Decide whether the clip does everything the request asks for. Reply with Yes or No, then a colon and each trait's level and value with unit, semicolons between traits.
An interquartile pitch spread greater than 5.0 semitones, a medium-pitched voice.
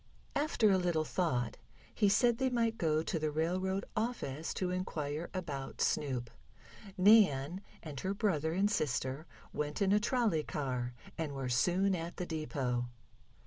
Yes: wide, 5.4 semitones; medium, 165 Hz